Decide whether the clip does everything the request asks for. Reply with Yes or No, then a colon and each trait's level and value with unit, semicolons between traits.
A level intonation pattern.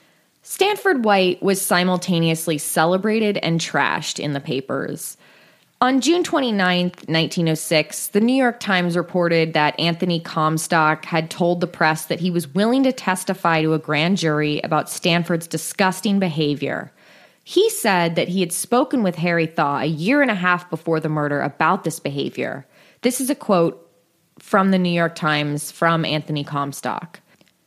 No: average, 3.4 semitones